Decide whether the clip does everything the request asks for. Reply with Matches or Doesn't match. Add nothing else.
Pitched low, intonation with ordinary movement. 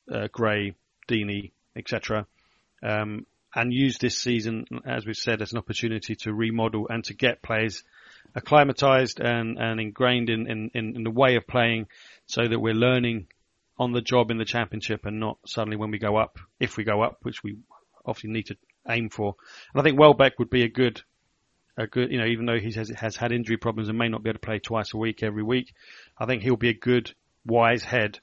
Doesn't match